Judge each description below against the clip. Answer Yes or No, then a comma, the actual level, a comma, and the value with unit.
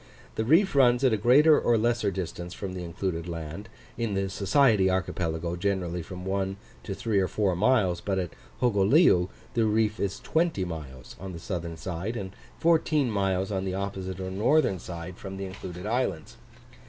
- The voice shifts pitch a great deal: No, average, 3.8 semitones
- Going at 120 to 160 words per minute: No, average, 180 wpm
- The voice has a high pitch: No, very low, 95 Hz